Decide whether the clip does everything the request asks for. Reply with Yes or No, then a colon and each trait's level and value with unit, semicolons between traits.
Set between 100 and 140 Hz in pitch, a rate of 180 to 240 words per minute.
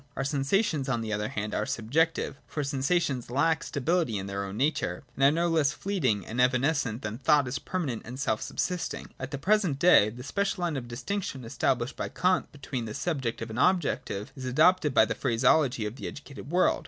Yes: low, 135 Hz; fast, 205 wpm